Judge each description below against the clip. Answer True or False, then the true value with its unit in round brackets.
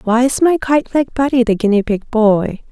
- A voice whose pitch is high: True (240 Hz)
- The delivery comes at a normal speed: False (220 wpm)